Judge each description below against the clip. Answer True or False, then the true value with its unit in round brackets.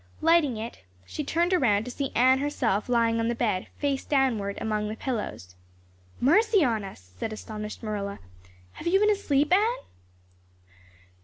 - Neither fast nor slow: True (155 wpm)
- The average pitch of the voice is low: False (245 Hz)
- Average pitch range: False (5.9 semitones)